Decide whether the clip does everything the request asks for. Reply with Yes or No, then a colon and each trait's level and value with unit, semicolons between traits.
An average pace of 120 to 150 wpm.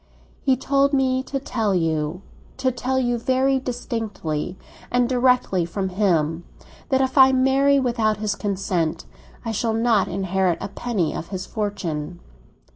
Yes: average, 140 wpm